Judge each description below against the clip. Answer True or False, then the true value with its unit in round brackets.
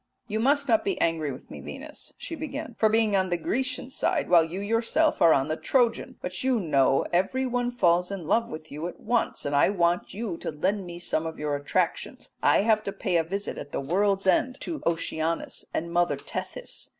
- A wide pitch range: True (6.1 semitones)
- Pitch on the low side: False (190 Hz)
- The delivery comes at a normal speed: False (215 wpm)